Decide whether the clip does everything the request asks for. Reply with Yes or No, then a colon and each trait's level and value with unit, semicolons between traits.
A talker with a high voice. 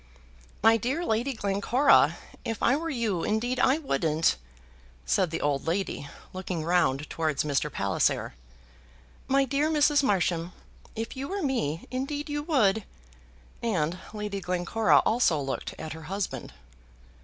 Yes: high, 210 Hz